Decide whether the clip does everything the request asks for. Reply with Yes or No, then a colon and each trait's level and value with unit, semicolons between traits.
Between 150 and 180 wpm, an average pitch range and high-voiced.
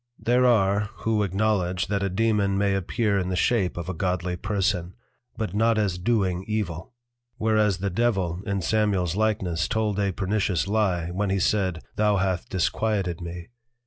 No: average, 165 wpm; average, 3.0 semitones; low, 100 Hz